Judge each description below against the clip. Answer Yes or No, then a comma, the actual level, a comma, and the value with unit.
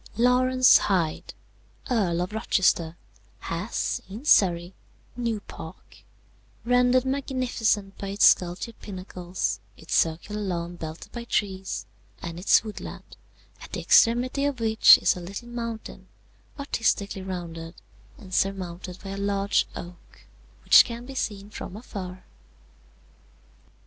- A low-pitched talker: No, high, 200 Hz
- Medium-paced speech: No, slow, 120 wpm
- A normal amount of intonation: Yes, average, 4.7 semitones